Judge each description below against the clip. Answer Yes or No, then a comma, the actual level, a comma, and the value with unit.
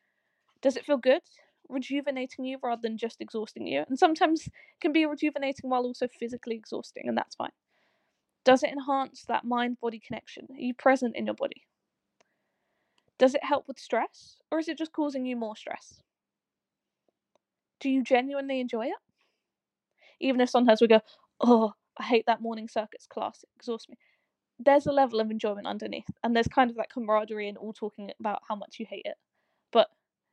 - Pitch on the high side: Yes, very high, 255 Hz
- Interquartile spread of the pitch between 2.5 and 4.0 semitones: Yes, average, 3.6 semitones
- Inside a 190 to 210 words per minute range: No, average, 180 wpm